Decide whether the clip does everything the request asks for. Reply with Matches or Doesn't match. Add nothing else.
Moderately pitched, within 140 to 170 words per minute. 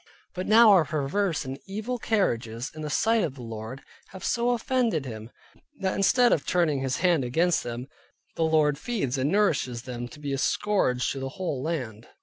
Doesn't match